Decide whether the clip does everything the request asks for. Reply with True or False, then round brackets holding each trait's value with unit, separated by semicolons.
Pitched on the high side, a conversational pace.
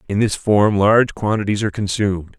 False (105 Hz; 175 wpm)